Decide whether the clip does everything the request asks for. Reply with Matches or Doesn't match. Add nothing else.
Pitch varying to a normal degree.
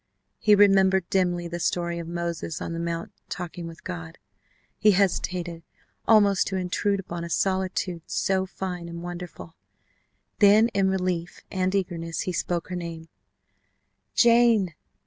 Doesn't match